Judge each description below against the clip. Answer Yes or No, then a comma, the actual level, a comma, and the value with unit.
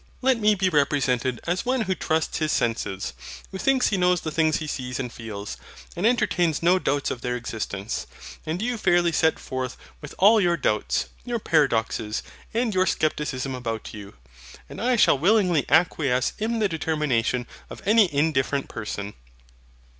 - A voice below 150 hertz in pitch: No, medium, 155 Hz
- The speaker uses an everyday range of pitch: No, wide, 7.1 semitones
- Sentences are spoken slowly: No, average, 165 wpm